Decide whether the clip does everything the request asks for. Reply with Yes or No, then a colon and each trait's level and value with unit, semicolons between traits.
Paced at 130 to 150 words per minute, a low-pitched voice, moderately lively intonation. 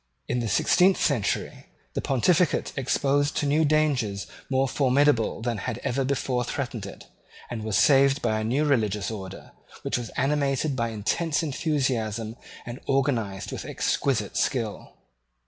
Yes: average, 140 wpm; low, 130 Hz; average, 4.2 semitones